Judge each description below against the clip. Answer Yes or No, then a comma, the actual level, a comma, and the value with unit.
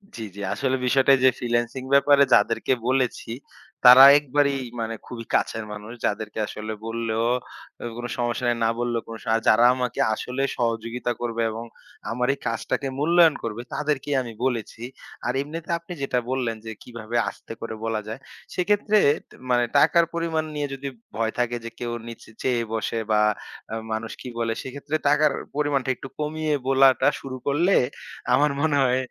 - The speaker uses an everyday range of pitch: Yes, average, 3.6 semitones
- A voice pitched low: Yes, low, 125 Hz